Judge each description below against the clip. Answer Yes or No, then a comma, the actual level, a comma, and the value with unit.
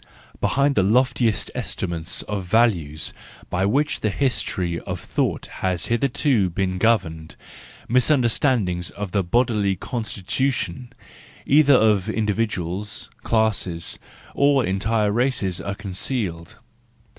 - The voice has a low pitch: Yes, low, 105 Hz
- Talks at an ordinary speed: No, slow, 110 wpm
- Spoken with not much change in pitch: No, average, 4.9 semitones